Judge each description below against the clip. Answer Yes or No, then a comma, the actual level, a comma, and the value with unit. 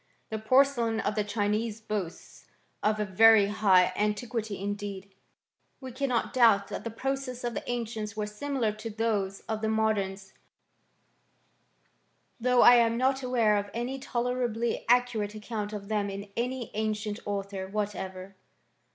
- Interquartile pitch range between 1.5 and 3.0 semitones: Yes, average, 2.7 semitones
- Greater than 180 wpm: No, average, 150 wpm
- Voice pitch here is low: No, high, 215 Hz